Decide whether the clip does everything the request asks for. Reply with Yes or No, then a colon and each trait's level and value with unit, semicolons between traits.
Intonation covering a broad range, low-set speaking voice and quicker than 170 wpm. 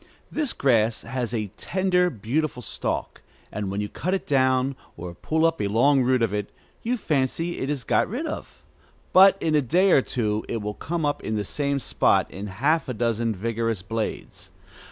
Yes: wide, 6.6 semitones; low, 130 Hz; average, 195 wpm